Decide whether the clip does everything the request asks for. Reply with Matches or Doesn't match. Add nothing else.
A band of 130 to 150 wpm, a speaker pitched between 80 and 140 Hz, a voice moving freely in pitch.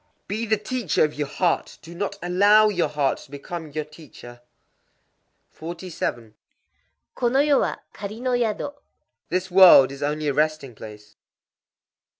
Doesn't match